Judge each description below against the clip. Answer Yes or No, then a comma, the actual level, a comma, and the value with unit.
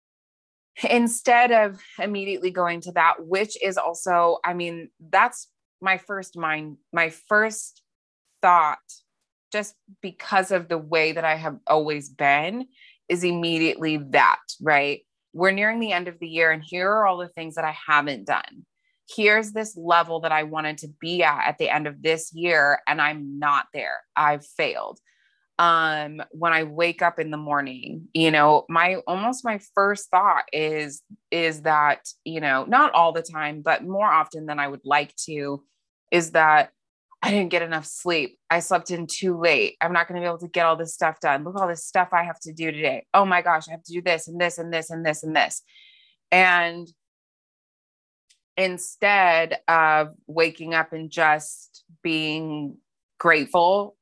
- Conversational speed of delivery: Yes, average, 180 wpm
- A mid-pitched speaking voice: Yes, medium, 165 Hz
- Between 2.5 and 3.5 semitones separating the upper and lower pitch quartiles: Yes, average, 2.9 semitones